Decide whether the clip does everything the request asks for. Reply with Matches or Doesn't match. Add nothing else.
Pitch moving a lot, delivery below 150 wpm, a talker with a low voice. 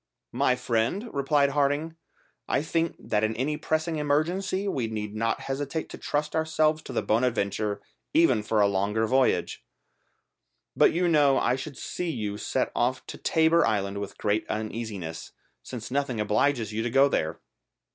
Doesn't match